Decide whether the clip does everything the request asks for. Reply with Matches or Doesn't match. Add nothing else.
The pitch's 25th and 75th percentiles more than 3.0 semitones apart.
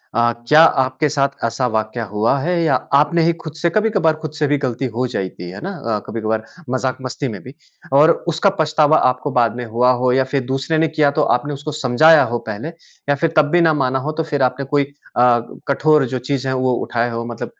Matches